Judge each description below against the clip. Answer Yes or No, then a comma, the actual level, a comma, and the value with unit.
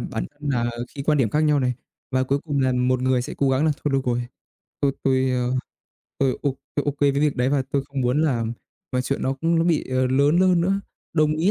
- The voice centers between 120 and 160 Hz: Yes, low, 135 Hz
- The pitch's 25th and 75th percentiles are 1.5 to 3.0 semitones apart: Yes, narrow, 2.6 semitones